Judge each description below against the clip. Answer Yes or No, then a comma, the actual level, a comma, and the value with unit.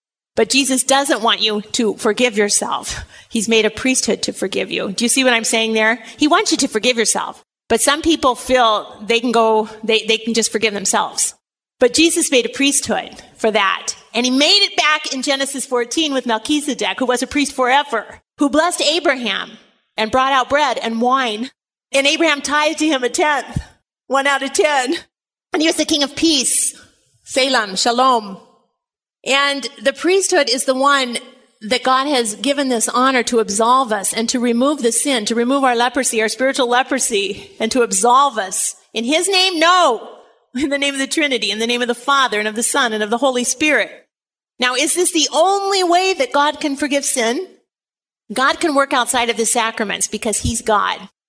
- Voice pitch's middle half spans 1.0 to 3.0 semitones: No, average, 3.8 semitones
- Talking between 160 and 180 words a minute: No, average, 200 wpm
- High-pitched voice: Yes, very high, 255 Hz